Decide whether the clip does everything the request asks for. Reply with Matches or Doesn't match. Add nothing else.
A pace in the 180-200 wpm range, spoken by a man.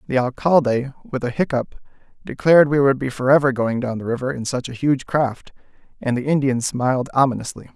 Matches